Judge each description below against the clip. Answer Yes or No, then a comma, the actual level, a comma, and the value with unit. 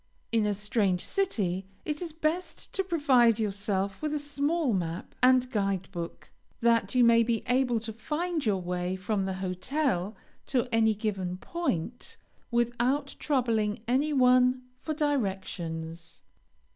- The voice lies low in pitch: No, high, 230 Hz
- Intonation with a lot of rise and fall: Yes, wide, 6.1 semitones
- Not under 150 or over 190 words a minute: No, average, 140 wpm